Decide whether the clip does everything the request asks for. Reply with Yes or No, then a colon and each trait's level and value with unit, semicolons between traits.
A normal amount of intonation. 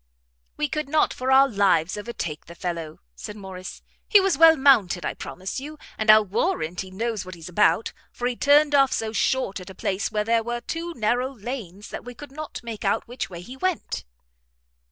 No: wide, 6.2 semitones